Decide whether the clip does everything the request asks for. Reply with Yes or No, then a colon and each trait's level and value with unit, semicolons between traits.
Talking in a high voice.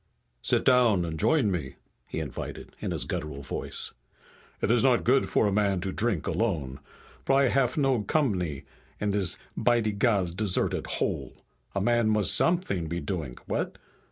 No: low, 105 Hz